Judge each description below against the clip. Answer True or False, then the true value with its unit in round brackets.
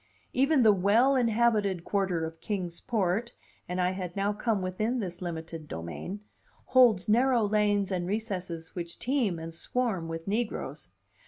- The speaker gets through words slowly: False (150 wpm)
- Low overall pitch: False (200 Hz)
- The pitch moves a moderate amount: True (4.5 semitones)